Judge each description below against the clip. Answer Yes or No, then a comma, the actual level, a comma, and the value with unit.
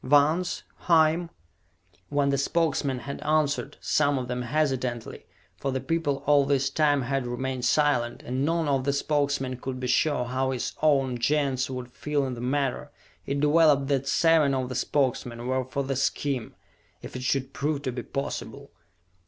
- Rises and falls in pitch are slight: Yes, narrow, 2.3 semitones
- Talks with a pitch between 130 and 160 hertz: Yes, medium, 140 Hz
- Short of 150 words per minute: No, average, 170 wpm